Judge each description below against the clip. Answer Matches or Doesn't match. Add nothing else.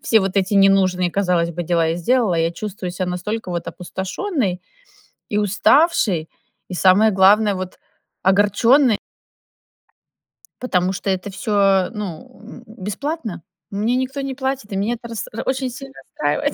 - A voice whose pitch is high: Matches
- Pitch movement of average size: Matches